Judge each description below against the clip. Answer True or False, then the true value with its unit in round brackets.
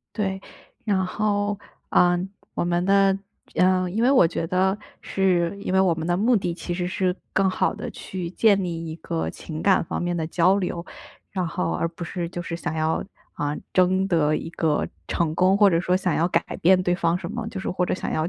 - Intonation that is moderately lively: False (2.2 semitones)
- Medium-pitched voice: True (180 Hz)